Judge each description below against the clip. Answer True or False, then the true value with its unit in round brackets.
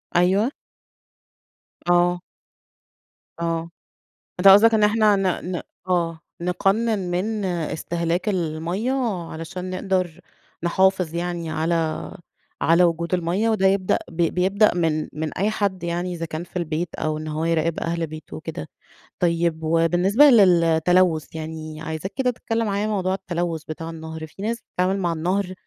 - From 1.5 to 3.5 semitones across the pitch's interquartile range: True (2.8 semitones)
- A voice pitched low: False (175 Hz)